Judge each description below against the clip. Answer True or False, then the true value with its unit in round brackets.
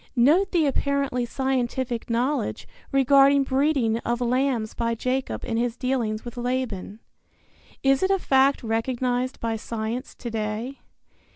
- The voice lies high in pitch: True (250 Hz)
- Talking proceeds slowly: True (130 wpm)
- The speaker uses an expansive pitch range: False (2.7 semitones)